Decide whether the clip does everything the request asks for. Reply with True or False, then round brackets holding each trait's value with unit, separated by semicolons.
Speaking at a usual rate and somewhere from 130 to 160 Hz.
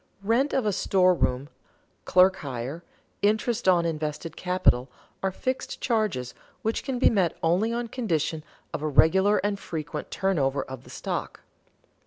False (145 wpm; 180 Hz)